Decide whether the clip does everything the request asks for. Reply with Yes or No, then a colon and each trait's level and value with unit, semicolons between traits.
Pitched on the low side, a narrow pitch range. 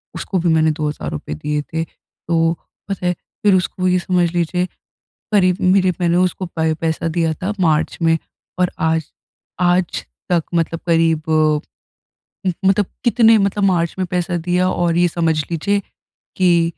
No: medium, 175 Hz; narrow, 2.1 semitones